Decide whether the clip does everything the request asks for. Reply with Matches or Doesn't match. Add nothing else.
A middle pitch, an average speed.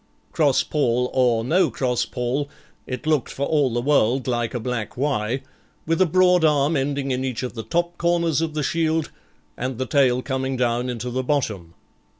Doesn't match